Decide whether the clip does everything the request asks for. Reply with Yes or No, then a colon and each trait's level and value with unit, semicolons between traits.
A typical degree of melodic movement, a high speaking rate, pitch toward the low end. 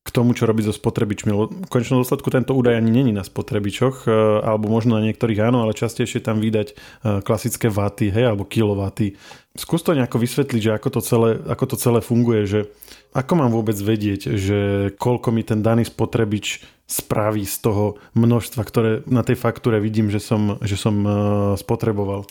No: narrow, 2.3 semitones; fast, 180 wpm; low, 110 Hz